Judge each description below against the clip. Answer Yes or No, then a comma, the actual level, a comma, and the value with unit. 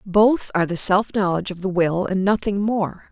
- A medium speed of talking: No, fast, 210 wpm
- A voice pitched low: No, high, 190 Hz